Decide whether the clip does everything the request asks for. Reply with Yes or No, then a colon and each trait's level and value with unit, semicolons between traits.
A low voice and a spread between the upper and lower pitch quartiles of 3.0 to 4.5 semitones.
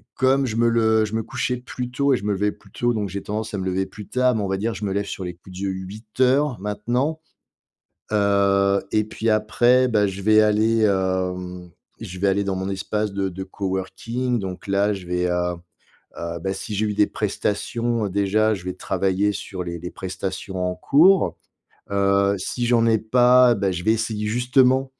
Yes: low, 105 Hz; average, 3.4 semitones